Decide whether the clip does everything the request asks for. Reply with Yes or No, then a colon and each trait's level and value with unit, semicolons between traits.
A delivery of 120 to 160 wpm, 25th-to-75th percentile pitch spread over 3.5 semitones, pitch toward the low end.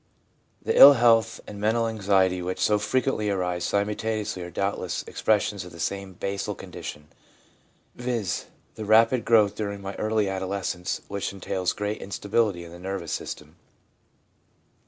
No: average, 150 wpm; average, 2.8 semitones; low, 100 Hz